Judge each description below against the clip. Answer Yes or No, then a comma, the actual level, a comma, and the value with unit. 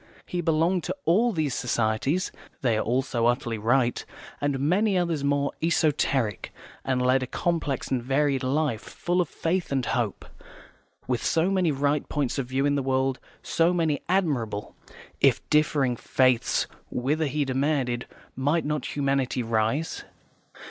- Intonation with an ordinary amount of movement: Yes, average, 3.9 semitones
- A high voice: No, medium, 140 Hz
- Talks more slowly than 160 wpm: Yes, average, 150 wpm